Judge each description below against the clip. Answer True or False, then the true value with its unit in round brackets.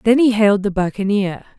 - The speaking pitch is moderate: False (205 Hz)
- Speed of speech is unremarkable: True (190 wpm)